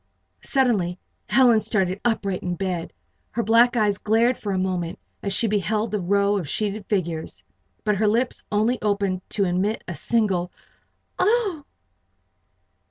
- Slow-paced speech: No, average, 145 wpm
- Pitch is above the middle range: Yes, high, 205 Hz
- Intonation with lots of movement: No, average, 3.5 semitones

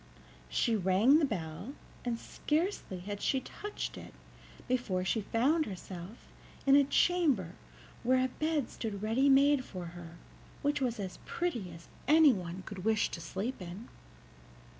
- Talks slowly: No, average, 145 wpm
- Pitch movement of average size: No, wide, 7.0 semitones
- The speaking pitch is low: No, high, 230 Hz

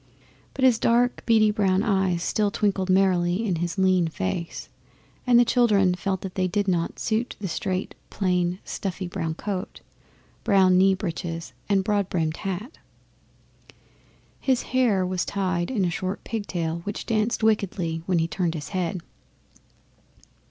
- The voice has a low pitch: No, high, 190 Hz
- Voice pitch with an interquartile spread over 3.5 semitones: No, average, 3.0 semitones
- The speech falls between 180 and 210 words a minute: No, average, 150 wpm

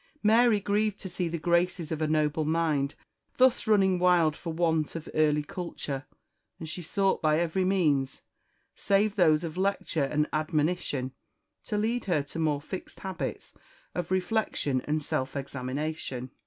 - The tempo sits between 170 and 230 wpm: No, average, 155 wpm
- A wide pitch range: No, average, 3.9 semitones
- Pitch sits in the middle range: Yes, medium, 165 Hz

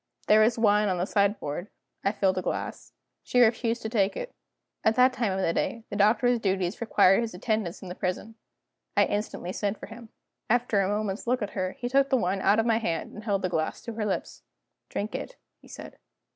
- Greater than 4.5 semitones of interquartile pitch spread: No, average, 3.2 semitones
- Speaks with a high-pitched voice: Yes, high, 210 Hz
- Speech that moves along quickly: Yes, fast, 220 wpm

